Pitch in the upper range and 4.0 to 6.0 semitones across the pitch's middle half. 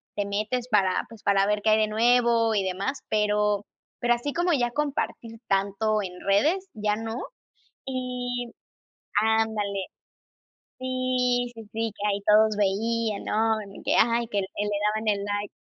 No: high, 220 Hz; average, 2.9 semitones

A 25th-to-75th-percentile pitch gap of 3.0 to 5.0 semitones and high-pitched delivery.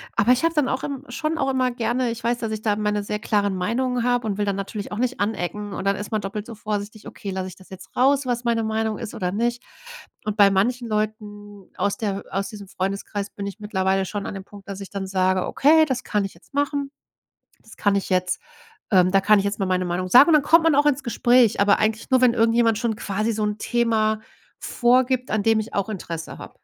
Yes: average, 3.5 semitones; high, 215 Hz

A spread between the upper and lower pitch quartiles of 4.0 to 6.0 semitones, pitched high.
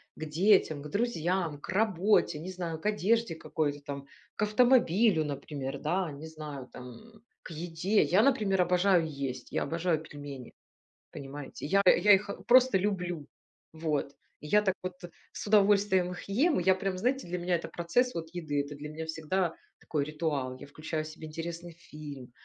No: average, 4.5 semitones; medium, 170 Hz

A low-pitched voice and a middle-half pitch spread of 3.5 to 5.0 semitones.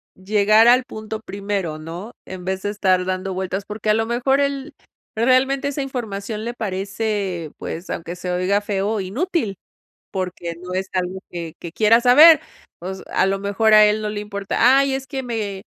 No: high, 205 Hz; average, 3.8 semitones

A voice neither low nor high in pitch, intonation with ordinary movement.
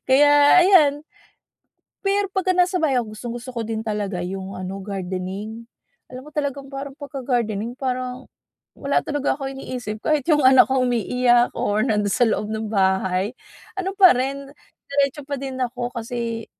No: very high, 250 Hz; average, 4.5 semitones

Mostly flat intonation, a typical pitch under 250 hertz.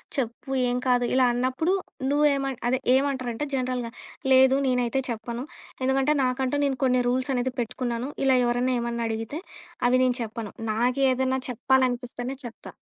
No: narrow, 1.5 semitones; very high, 255 Hz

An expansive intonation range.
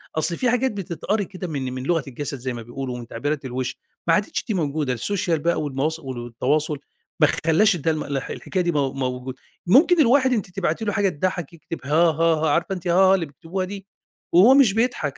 Yes: wide, 5.8 semitones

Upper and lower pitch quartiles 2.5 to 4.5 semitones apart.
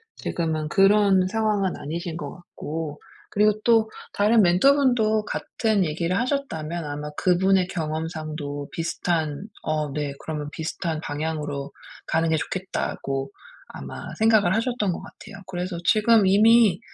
No: average, 5.2 semitones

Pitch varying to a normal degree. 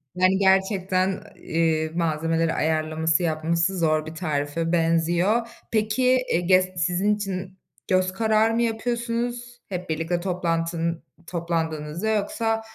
Yes: average, 4.2 semitones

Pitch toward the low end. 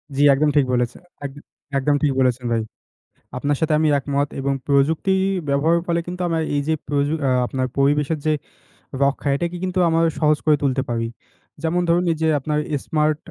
No: medium, 145 Hz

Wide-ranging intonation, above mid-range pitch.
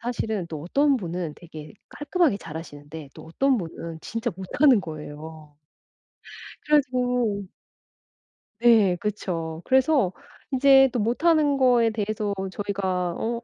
Yes: wide, 7.5 semitones; high, 205 Hz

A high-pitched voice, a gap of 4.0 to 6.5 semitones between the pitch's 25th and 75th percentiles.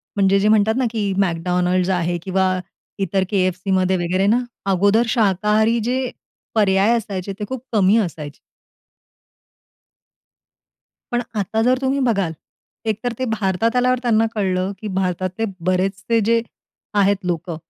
No: high, 195 Hz; average, 3.3 semitones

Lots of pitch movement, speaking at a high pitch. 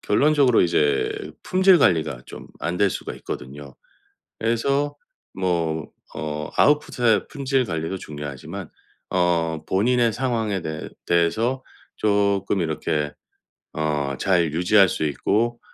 No: wide, 7.1 semitones; very low, 95 Hz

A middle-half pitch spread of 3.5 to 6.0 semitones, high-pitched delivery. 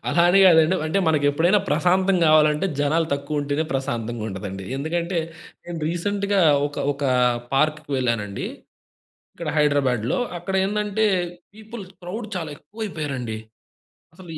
No: average, 4.9 semitones; medium, 155 Hz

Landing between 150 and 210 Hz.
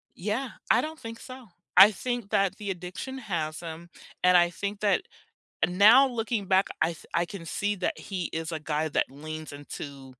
Yes: high, 190 Hz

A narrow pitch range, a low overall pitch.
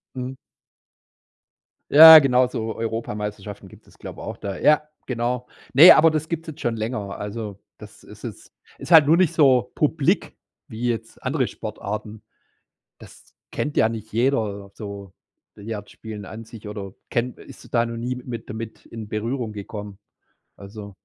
No: average, 3.4 semitones; low, 115 Hz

